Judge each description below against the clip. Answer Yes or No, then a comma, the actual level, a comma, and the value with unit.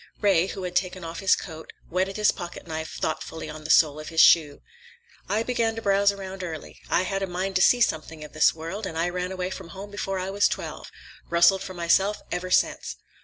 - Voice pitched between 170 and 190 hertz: Yes, medium, 185 Hz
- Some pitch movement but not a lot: Yes, average, 3.0 semitones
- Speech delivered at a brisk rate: Yes, fast, 220 wpm